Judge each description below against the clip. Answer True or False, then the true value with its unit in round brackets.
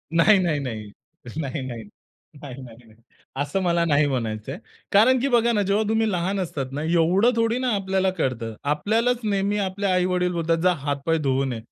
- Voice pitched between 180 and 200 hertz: False (170 Hz)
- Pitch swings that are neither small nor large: False (6.6 semitones)